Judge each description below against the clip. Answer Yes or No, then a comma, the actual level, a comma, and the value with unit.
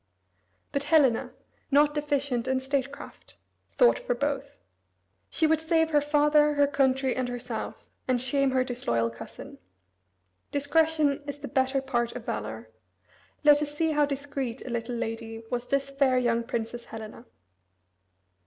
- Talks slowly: No, average, 145 wpm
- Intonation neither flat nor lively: Yes, average, 3.4 semitones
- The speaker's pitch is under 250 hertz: No, very high, 270 Hz